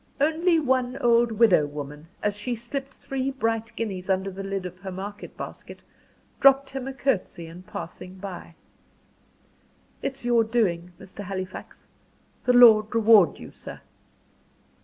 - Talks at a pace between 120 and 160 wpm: Yes, average, 140 wpm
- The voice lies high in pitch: Yes, high, 220 Hz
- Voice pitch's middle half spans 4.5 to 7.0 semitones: Yes, average, 5.1 semitones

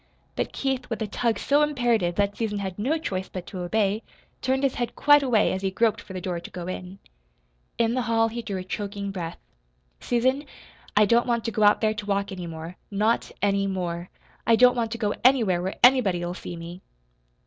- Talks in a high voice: Yes, high, 205 Hz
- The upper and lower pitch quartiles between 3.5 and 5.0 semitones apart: Yes, average, 4.1 semitones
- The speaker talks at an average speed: No, fast, 215 wpm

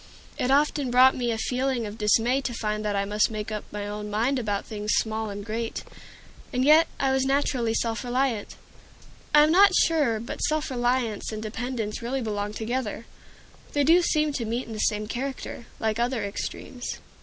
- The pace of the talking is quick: No, average, 190 wpm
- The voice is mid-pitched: No, high, 235 Hz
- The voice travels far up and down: No, average, 3.7 semitones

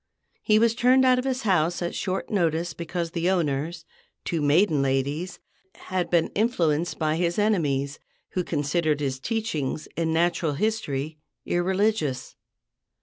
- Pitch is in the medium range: Yes, medium, 170 Hz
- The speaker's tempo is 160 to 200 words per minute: No, average, 140 wpm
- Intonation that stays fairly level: No, average, 4.4 semitones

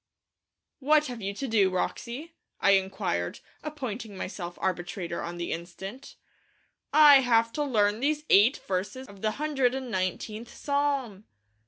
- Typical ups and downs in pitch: No, wide, 6.1 semitones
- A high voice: Yes, high, 225 Hz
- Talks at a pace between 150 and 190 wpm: No, average, 140 wpm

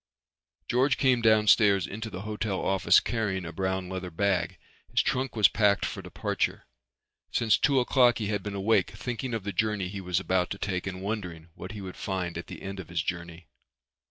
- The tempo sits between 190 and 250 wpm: Yes, average, 195 wpm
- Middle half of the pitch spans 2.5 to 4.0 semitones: Yes, average, 3.1 semitones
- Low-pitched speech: Yes, low, 100 Hz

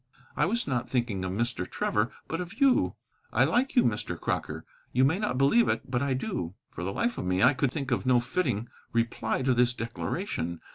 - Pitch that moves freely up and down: Yes, wide, 6.8 semitones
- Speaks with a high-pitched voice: No, low, 125 Hz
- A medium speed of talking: No, fast, 210 wpm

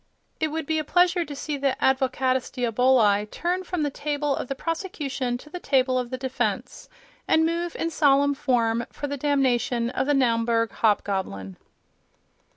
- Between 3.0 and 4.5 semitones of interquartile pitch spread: Yes, average, 3.7 semitones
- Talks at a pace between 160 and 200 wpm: Yes, average, 165 wpm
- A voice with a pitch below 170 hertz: No, very high, 270 Hz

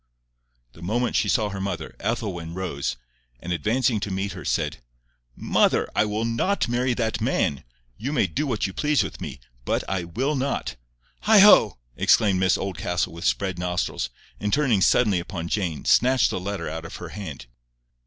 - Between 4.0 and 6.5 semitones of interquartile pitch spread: Yes, average, 5.2 semitones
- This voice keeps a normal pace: Yes, average, 175 wpm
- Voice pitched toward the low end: Yes, low, 100 Hz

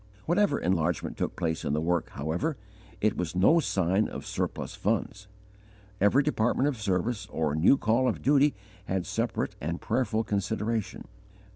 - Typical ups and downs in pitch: No, wide, 6.4 semitones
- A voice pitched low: Yes, low, 105 Hz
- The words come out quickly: No, average, 150 wpm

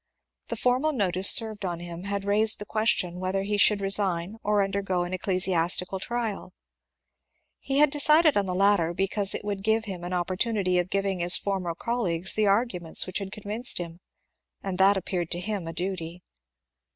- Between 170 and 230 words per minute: Yes, average, 180 wpm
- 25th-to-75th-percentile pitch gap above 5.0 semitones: No, average, 2.7 semitones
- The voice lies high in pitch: Yes, high, 195 Hz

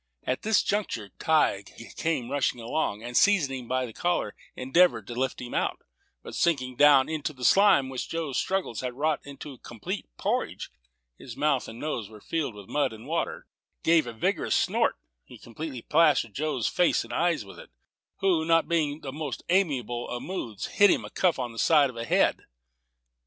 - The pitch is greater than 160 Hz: No, low, 135 Hz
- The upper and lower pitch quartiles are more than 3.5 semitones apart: Yes, average, 5.1 semitones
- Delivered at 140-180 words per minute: No, average, 195 wpm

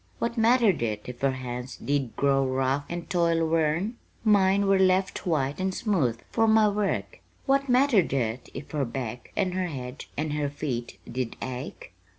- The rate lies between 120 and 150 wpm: No, average, 170 wpm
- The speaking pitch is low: No, medium, 155 Hz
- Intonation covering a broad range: Yes, wide, 7.1 semitones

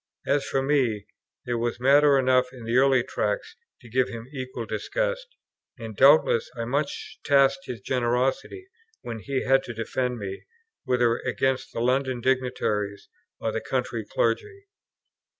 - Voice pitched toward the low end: Yes, low, 130 Hz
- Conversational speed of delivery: Yes, average, 150 wpm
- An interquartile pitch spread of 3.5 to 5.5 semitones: No, average, 2.7 semitones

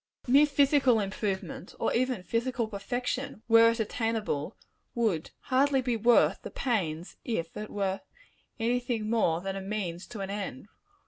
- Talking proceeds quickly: No, average, 150 wpm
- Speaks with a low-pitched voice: No, high, 225 Hz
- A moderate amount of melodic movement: Yes, average, 4.0 semitones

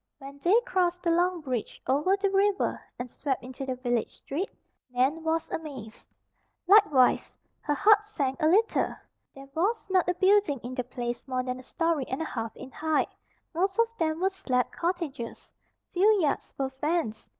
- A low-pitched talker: No, very high, 315 Hz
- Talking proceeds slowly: No, average, 175 wpm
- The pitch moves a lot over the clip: Yes, wide, 6.2 semitones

